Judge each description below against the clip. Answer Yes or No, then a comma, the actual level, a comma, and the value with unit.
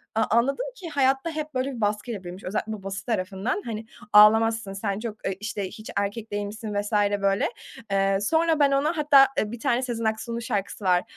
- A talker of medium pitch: No, high, 220 Hz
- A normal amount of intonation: Yes, average, 4.2 semitones